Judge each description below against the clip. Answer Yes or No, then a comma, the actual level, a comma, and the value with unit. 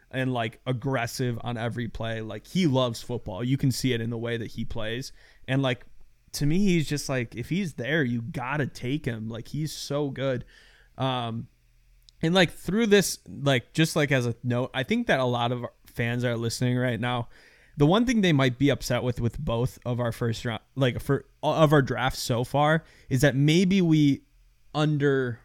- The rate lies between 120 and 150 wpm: No, fast, 205 wpm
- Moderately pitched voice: No, low, 125 Hz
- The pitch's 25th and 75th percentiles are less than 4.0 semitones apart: Yes, average, 3.4 semitones